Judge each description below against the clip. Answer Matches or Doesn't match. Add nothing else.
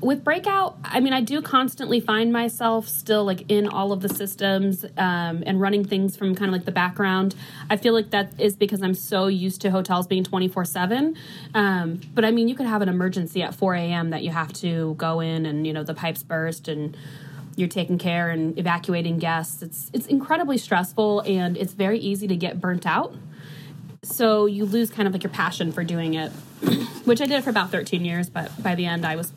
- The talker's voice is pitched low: Doesn't match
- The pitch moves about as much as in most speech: Matches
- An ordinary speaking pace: Doesn't match